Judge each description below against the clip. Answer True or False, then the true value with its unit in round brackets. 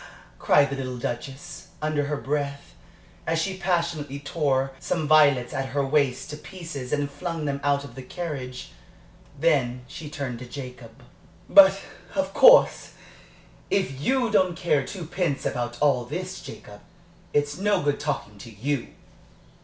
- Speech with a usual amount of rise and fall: True (3.8 semitones)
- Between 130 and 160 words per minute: True (145 wpm)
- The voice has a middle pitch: True (145 Hz)